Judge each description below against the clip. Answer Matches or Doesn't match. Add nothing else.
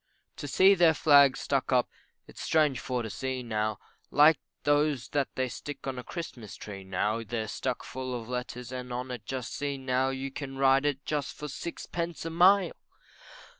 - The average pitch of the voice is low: Matches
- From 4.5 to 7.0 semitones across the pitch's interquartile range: Doesn't match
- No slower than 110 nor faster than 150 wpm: Doesn't match